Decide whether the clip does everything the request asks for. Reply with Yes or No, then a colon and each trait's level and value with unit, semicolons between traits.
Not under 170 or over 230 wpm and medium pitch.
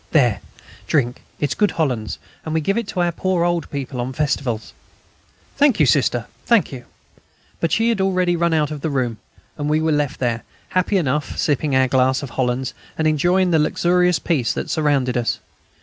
Yes: average, 190 wpm; medium, 150 Hz